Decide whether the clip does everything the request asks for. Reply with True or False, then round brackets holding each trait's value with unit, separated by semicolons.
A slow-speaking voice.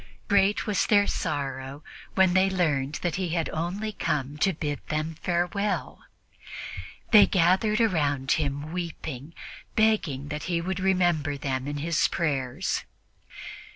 True (130 wpm)